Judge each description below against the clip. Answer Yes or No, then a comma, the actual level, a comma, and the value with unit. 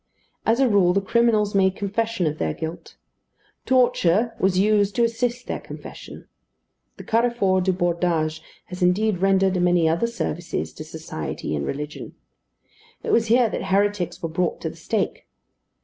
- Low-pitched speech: No, high, 190 Hz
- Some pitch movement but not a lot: Yes, average, 4.6 semitones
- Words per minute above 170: No, average, 155 wpm